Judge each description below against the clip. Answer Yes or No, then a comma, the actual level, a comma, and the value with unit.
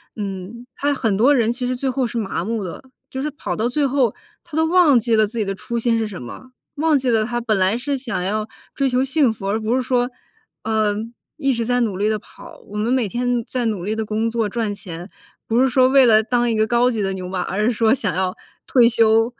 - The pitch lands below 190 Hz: No, high, 230 Hz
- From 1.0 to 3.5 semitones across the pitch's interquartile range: Yes, average, 2.9 semitones